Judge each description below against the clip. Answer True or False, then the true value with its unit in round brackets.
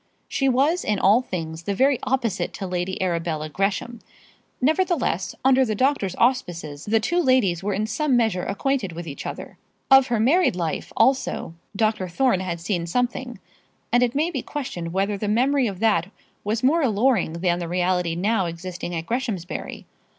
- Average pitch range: False (6.4 semitones)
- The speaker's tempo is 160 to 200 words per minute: True (170 wpm)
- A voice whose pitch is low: False (210 Hz)